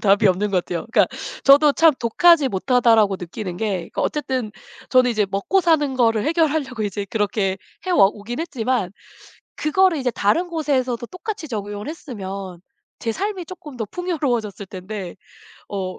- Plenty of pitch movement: Yes, wide, 7.1 semitones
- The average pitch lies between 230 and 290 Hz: Yes, high, 235 Hz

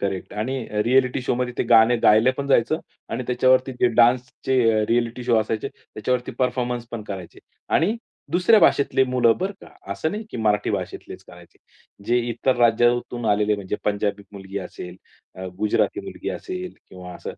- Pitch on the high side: No, low, 120 Hz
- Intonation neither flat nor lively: Yes, average, 3.3 semitones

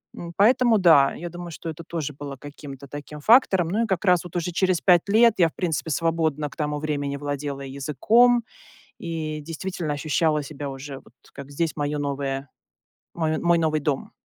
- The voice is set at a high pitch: No, medium, 155 Hz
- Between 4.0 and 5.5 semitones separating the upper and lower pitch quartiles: No, average, 3.3 semitones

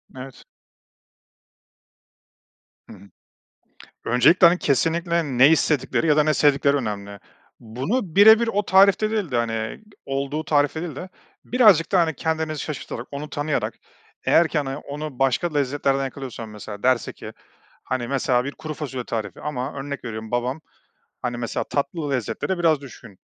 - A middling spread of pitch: Yes, average, 4.4 semitones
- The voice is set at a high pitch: No, medium, 140 Hz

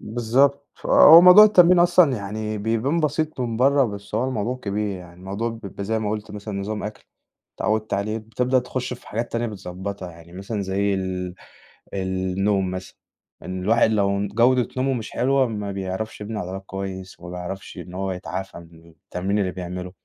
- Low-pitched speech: Yes, low, 105 Hz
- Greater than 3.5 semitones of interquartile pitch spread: Yes, average, 3.9 semitones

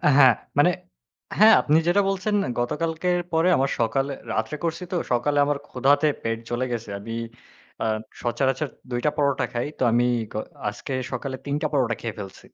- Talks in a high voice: No, low, 135 Hz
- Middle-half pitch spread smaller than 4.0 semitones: No, average, 4.5 semitones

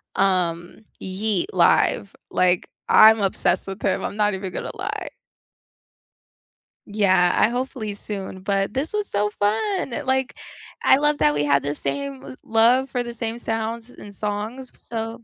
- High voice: Yes, high, 210 Hz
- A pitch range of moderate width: Yes, average, 3.9 semitones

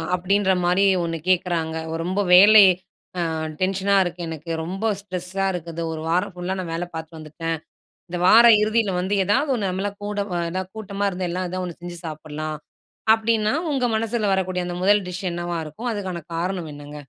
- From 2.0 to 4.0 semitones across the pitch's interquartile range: Yes, average, 3.1 semitones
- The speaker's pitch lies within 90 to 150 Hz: No, medium, 185 Hz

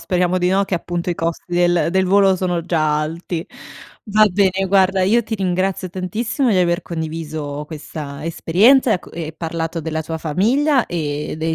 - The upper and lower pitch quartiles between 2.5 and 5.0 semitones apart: Yes, average, 2.9 semitones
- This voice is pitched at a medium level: Yes, medium, 175 Hz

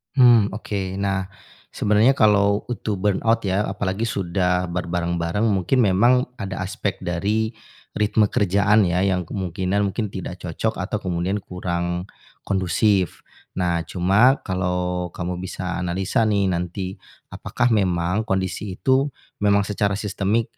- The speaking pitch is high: No, very low, 95 Hz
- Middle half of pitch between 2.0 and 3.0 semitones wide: Yes, narrow, 2.6 semitones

